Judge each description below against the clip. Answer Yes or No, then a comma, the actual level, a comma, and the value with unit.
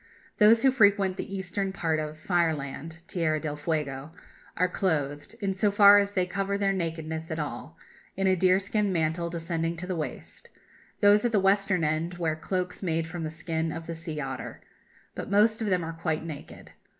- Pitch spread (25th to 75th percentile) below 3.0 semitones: No, average, 3.5 semitones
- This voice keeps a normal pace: Yes, average, 185 wpm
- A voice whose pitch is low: No, medium, 170 Hz